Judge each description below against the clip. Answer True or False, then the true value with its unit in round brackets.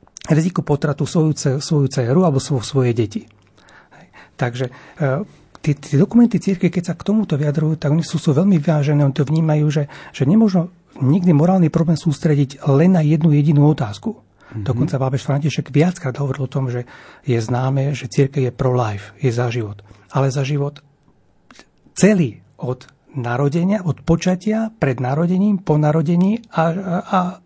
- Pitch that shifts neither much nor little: True (3.9 semitones)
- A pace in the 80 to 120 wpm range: False (155 wpm)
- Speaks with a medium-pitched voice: True (150 Hz)